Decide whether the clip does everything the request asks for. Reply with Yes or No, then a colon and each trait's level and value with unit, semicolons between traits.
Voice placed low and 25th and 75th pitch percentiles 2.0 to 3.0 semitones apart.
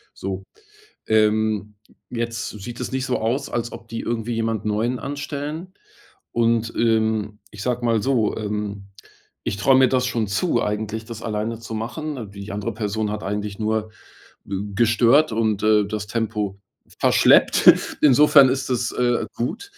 Yes: low, 110 Hz; narrow, 2.6 semitones